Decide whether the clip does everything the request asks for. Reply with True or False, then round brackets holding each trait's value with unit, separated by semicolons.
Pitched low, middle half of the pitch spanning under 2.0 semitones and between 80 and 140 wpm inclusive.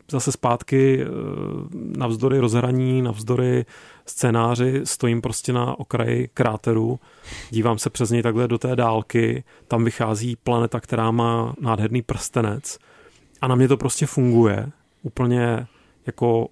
True (120 Hz; 1.6 semitones; 125 wpm)